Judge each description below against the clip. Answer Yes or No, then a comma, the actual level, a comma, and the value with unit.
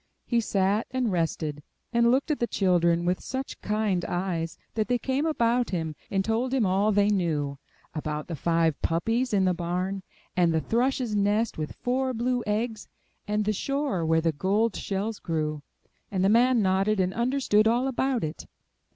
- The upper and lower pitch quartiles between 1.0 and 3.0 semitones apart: No, wide, 5.5 semitones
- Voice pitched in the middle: No, high, 205 Hz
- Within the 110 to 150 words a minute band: No, average, 175 wpm